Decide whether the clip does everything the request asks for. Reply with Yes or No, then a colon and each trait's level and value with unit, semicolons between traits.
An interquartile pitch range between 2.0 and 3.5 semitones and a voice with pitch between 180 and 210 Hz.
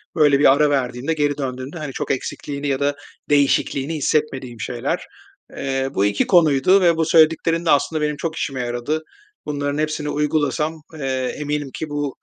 No: narrow, 2.4 semitones; medium, 145 Hz